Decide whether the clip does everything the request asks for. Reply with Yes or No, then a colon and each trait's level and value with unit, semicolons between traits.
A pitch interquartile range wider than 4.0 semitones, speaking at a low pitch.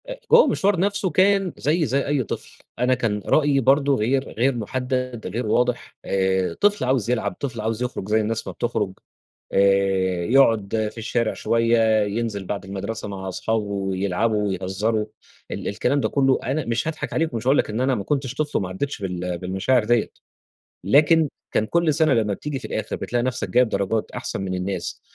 Yes: average, 5.1 semitones; low, 115 Hz